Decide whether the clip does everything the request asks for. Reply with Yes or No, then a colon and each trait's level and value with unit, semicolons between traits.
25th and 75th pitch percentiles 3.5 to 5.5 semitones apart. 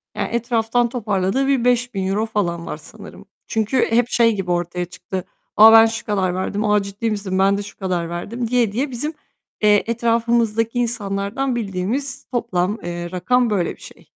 Yes: average, 3.8 semitones